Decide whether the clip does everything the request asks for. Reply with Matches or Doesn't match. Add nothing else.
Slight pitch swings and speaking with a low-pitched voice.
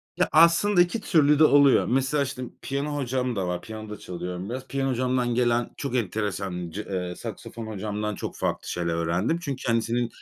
Doesn't match